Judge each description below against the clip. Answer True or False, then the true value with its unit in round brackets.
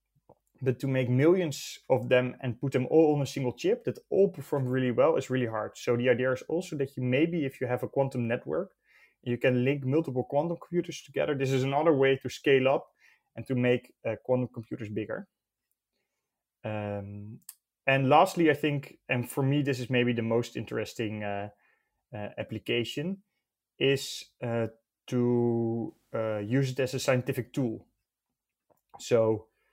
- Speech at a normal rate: True (170 wpm)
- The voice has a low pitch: True (130 Hz)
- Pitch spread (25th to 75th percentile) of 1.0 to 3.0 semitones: True (2.7 semitones)